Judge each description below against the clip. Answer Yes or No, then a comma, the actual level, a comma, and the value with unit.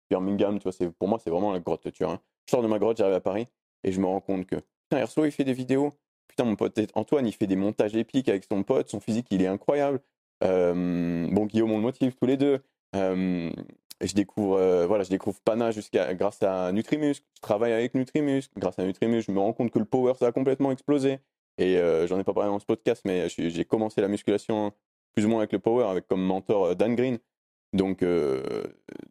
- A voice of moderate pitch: No, low, 105 Hz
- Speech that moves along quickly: Yes, fast, 245 wpm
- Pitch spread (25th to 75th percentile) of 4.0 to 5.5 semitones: Yes, average, 4.7 semitones